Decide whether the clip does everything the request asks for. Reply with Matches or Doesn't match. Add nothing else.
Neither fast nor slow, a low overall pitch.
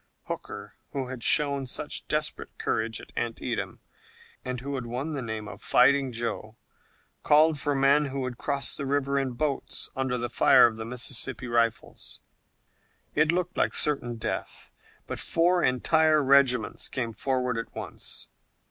Matches